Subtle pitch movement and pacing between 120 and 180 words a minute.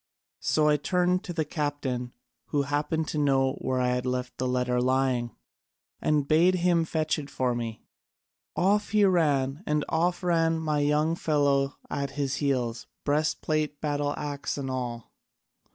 No: average, 3.3 semitones; average, 160 wpm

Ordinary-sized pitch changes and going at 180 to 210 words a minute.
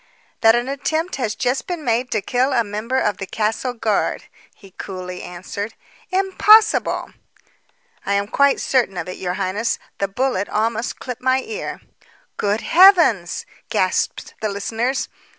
No: average, 4.8 semitones; average, 150 wpm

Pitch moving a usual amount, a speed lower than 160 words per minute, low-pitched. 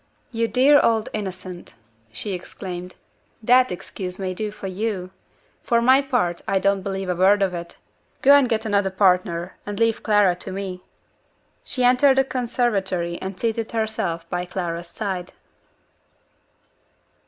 No: average, 4.0 semitones; average, 145 wpm; high, 195 Hz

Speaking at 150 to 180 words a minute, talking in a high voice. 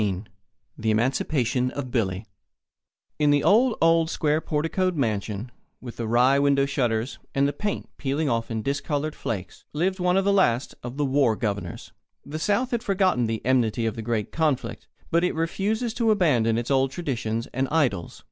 No: average, 175 wpm; low, 135 Hz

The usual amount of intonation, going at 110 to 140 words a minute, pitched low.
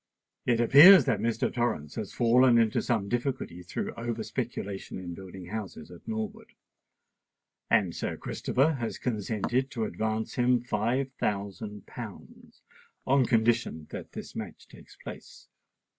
Yes: average, 3.2 semitones; slow, 135 wpm; low, 115 Hz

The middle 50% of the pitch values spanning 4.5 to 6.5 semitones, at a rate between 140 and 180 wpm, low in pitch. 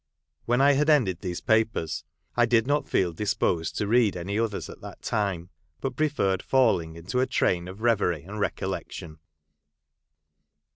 Yes: wide, 5.6 semitones; average, 160 wpm; low, 105 Hz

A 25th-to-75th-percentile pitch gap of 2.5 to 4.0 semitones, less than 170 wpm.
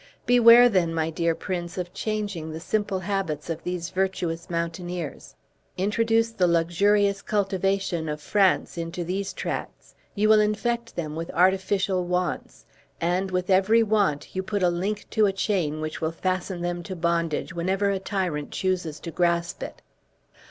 Yes: average, 3.0 semitones; average, 160 wpm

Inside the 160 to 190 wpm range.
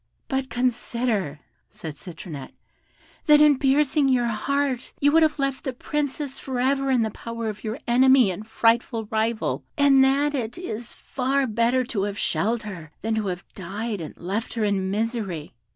Yes: average, 170 wpm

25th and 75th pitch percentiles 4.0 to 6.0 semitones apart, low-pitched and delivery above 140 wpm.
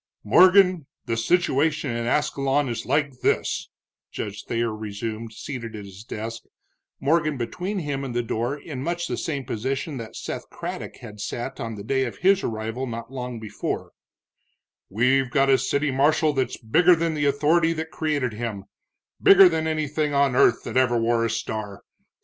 Yes: average, 4.9 semitones; low, 130 Hz; average, 170 wpm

